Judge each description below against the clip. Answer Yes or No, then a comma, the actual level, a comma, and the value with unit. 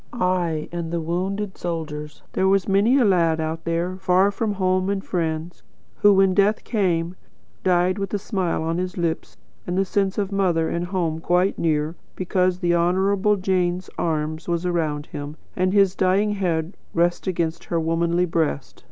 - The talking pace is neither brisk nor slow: Yes, average, 170 wpm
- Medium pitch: Yes, medium, 180 Hz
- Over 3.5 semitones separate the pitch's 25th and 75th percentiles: No, narrow, 2.5 semitones